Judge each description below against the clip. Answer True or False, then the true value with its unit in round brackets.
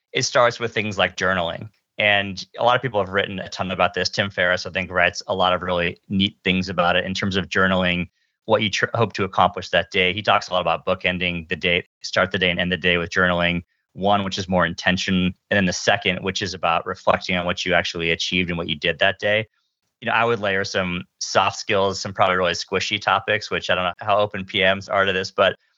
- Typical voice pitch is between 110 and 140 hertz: False (95 Hz)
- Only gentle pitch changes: True (1.8 semitones)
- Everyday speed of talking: False (250 wpm)